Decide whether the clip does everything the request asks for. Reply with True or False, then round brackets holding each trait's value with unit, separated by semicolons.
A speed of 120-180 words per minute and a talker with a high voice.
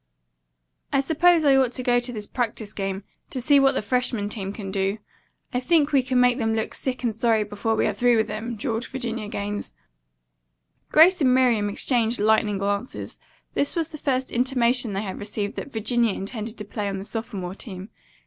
False (195 wpm; 230 Hz)